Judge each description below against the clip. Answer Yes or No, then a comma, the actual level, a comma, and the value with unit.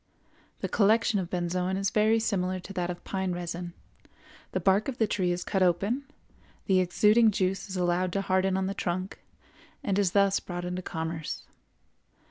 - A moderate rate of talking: Yes, average, 175 wpm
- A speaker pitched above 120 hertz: Yes, high, 190 Hz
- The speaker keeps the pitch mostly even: Yes, narrow, 2.1 semitones